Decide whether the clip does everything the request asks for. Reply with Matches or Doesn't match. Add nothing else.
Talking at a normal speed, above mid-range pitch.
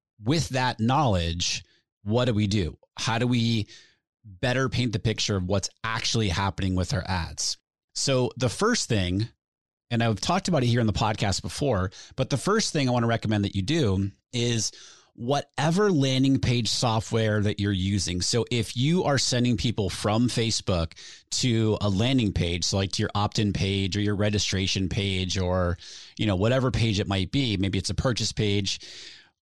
Doesn't match